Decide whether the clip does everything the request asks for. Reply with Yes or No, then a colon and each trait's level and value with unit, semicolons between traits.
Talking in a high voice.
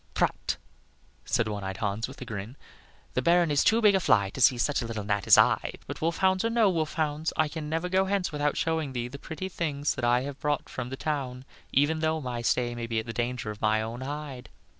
No: medium, 140 Hz